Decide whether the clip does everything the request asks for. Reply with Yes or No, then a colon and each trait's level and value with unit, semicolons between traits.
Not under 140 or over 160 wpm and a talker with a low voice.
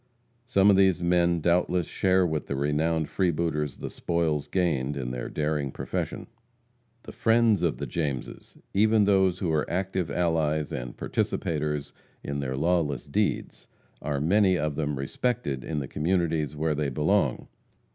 Yes: average, 150 wpm; very low, 80 Hz